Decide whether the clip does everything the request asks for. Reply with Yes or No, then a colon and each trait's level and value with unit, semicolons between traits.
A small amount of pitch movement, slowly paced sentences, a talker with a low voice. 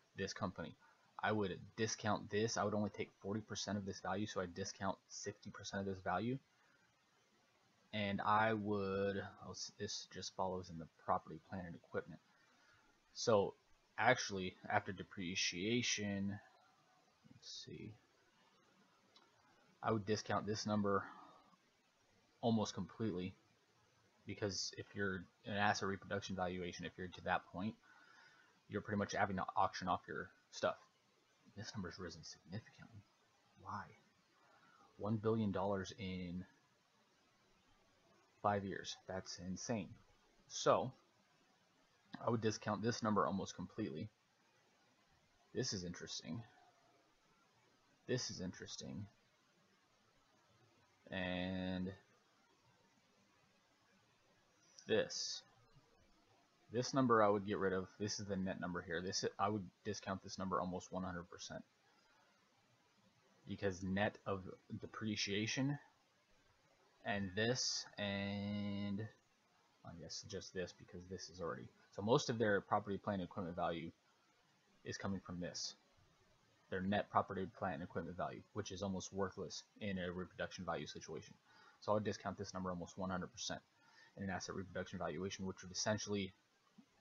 Yes: narrow, 2.0 semitones; slow, 125 wpm; low, 100 Hz